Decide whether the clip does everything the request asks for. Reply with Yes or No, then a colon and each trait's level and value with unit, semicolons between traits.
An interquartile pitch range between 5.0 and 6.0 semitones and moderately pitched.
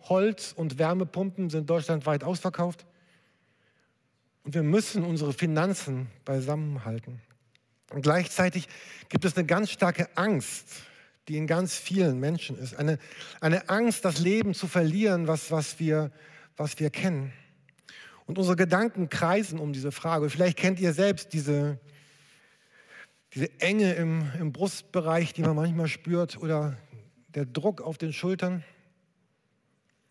No: average, 3.4 semitones; medium, 165 Hz